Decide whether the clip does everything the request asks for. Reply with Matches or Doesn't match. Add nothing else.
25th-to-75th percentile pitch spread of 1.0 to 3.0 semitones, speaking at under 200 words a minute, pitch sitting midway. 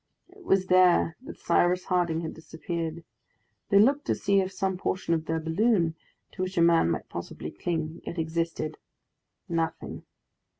Matches